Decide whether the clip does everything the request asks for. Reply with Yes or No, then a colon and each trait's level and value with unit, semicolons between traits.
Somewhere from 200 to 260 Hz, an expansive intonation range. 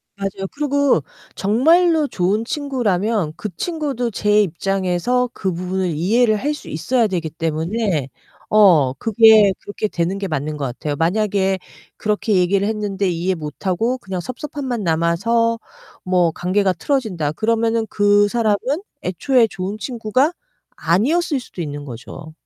No: high, 205 Hz; average, 4.8 semitones